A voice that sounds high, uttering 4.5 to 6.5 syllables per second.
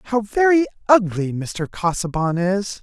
No: high, 200 Hz; 4.3 syllables/s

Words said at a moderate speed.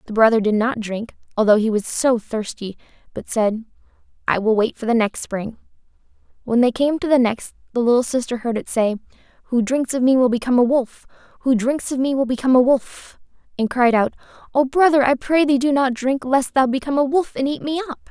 No: fast, 220 wpm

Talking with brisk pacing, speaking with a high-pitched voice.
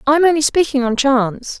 Yes: fast, 225 wpm; very high, 275 Hz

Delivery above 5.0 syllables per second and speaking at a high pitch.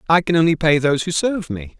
No: 6.8 syllables/s; medium, 160 Hz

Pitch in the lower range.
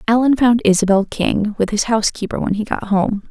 No: high, 215 Hz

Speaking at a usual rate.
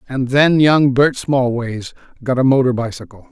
Yes: average, 165 wpm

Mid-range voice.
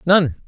Yes: medium, 175 Hz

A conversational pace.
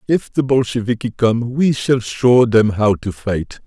Yes: average, 180 wpm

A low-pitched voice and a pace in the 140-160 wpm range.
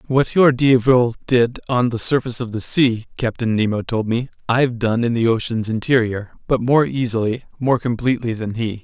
No: low, 120 Hz; average, 185 wpm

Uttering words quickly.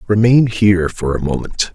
No: average, 170 wpm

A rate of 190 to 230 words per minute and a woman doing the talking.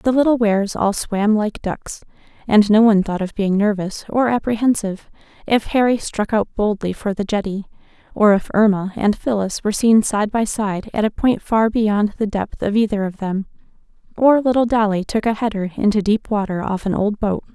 Yes: average, 200 wpm; female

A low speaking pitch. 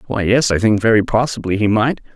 Yes: low, 110 Hz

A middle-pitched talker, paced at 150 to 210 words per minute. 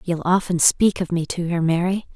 No: medium, 175 Hz; fast, 225 wpm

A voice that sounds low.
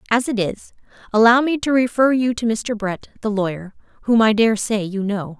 No: high, 220 Hz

